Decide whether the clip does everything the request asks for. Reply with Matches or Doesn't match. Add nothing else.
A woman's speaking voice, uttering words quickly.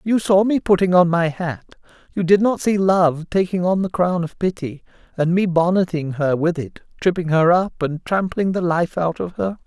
Doesn't match